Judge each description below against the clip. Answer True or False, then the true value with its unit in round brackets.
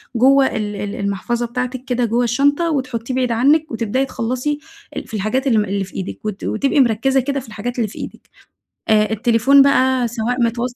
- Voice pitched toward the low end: False (240 Hz)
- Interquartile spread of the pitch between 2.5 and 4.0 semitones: True (3.1 semitones)